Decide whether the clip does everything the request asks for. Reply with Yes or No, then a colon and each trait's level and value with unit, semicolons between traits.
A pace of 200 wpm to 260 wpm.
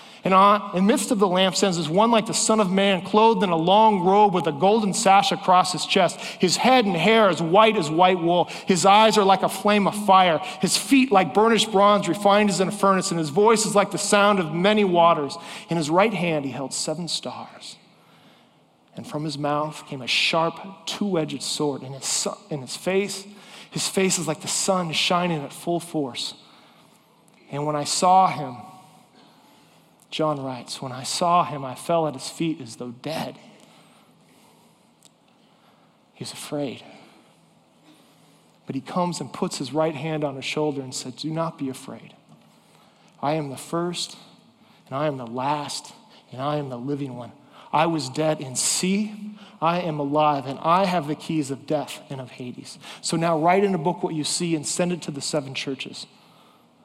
No: average, 190 wpm